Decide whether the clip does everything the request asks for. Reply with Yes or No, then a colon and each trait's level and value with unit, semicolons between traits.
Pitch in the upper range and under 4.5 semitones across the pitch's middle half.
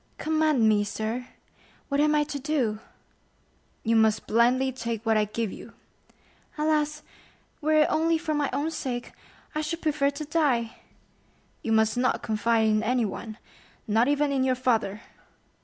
No: very high, 255 Hz; average, 5.2 semitones